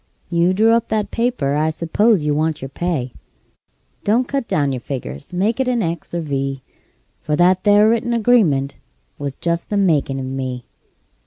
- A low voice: No, medium, 170 Hz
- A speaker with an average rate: Yes, average, 180 wpm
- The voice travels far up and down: Yes, wide, 7.7 semitones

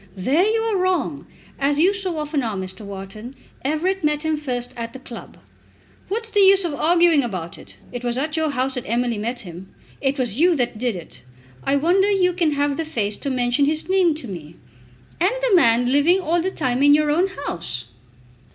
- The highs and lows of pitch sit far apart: Yes, wide, 6.3 semitones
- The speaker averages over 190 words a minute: Yes, fast, 205 wpm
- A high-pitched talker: Yes, very high, 285 Hz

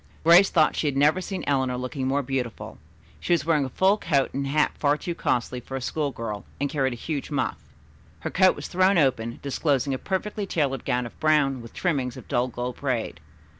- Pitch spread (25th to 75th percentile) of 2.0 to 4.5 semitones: Yes, average, 3.8 semitones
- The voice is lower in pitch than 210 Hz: Yes, medium, 140 Hz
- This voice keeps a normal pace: No, fast, 210 wpm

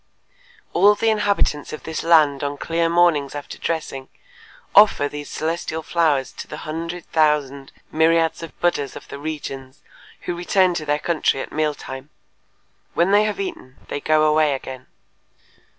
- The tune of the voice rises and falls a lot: No, average, 3.0 semitones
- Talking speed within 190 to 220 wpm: No, average, 155 wpm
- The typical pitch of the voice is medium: Yes, medium, 155 Hz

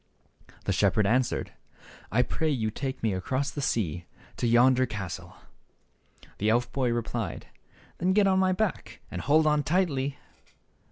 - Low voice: Yes, low, 130 Hz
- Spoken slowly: No, average, 150 wpm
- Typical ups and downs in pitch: Yes, average, 5.0 semitones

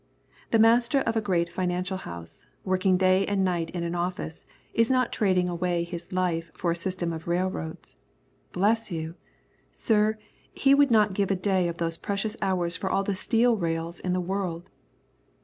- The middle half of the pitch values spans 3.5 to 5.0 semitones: No, average, 3.1 semitones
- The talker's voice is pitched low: No, medium, 185 Hz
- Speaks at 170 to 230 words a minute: Yes, average, 180 wpm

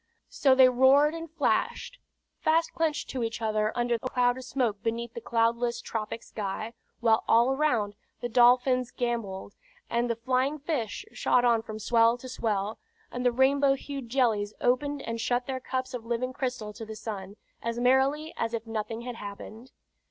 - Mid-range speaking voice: No, high, 240 Hz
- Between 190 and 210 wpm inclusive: No, average, 175 wpm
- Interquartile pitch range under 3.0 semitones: Yes, narrow, 2.5 semitones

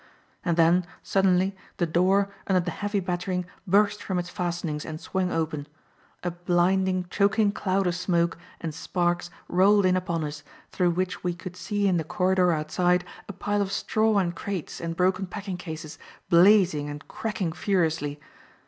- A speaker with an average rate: Yes, average, 165 wpm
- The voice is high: No, medium, 180 Hz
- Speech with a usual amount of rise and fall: No, narrow, 2.2 semitones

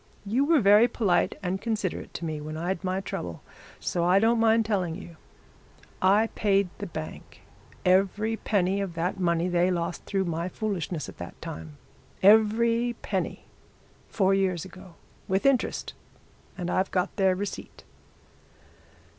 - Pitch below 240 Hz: Yes, high, 190 Hz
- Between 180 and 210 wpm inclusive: No, average, 145 wpm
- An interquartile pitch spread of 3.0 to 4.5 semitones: Yes, average, 3.4 semitones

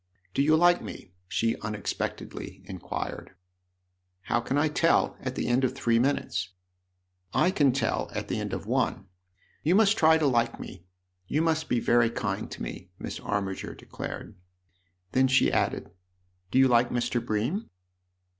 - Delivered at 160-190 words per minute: Yes, average, 180 wpm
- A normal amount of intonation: No, wide, 7.3 semitones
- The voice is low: Yes, low, 120 Hz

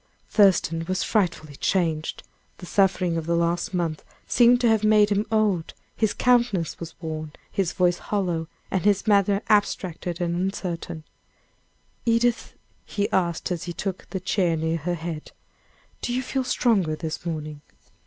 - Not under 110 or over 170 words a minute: Yes, average, 155 wpm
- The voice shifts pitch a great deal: No, average, 3.7 semitones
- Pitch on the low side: No, medium, 180 Hz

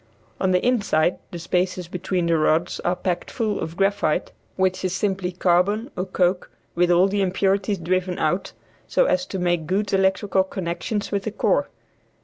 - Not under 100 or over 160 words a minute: No, average, 170 wpm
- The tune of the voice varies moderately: No, narrow, 2.0 semitones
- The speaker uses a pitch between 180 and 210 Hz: Yes, medium, 185 Hz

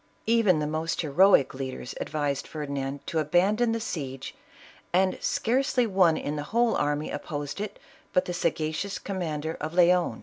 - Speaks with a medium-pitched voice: Yes, medium, 160 Hz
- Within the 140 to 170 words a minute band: Yes, average, 165 wpm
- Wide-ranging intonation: No, average, 4.8 semitones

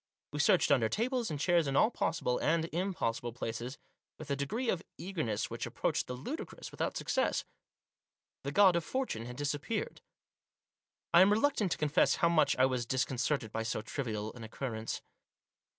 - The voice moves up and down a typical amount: No, wide, 7.0 semitones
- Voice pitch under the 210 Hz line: Yes, medium, 140 Hz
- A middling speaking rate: Yes, average, 170 wpm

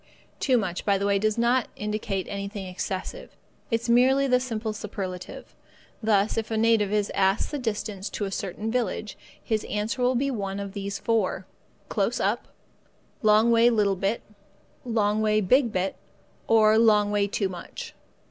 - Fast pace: No, average, 165 wpm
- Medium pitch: No, high, 215 Hz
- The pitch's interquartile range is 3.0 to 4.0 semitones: No, narrow, 2.5 semitones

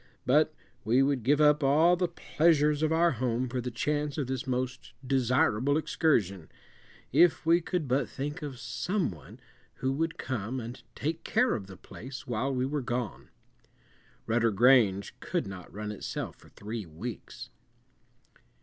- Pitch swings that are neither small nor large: Yes, average, 4.5 semitones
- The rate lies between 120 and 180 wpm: Yes, average, 160 wpm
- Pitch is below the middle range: Yes, low, 130 Hz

